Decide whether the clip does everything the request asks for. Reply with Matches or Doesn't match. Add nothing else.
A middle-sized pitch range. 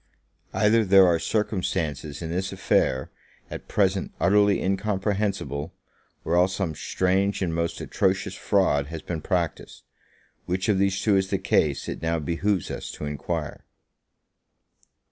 Matches